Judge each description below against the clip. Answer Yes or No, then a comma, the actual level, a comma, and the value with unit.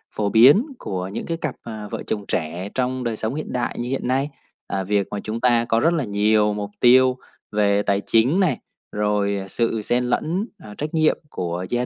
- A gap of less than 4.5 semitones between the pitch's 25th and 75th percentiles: Yes, average, 4.0 semitones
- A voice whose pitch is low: Yes, low, 115 Hz